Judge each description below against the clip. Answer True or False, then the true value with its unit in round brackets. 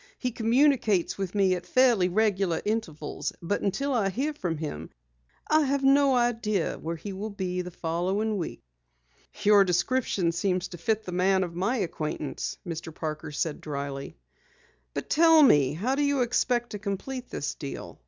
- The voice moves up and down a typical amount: False (6.2 semitones)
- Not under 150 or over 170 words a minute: True (165 wpm)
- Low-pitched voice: False (195 Hz)